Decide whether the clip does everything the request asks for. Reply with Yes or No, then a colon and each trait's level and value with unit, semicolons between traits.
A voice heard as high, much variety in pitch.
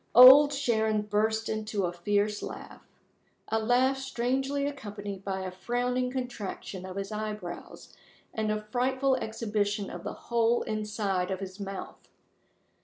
No: high, 215 Hz; average, 3.5 semitones